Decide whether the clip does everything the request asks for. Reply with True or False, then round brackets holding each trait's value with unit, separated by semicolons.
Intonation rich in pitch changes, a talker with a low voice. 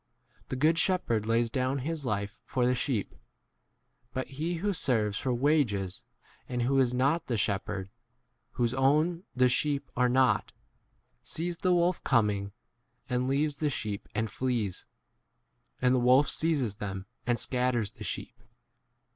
False (4.5 semitones; 125 Hz)